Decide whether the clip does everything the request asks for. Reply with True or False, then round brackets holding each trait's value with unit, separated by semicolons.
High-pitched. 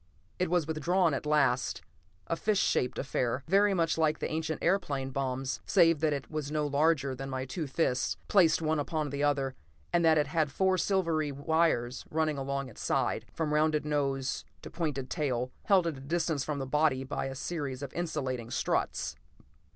False (150 Hz)